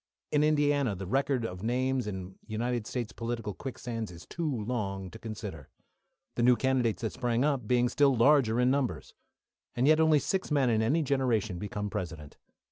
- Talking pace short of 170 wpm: No, average, 175 wpm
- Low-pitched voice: Yes, low, 120 Hz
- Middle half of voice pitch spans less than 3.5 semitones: No, average, 4.2 semitones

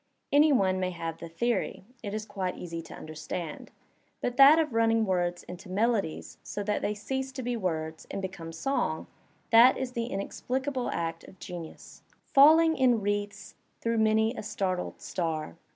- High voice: Yes, high, 205 Hz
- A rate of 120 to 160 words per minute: No, average, 175 wpm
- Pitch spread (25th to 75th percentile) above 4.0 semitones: Yes, wide, 5.4 semitones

